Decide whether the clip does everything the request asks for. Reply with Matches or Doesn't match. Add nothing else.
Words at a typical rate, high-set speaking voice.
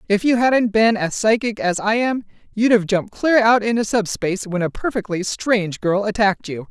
Matches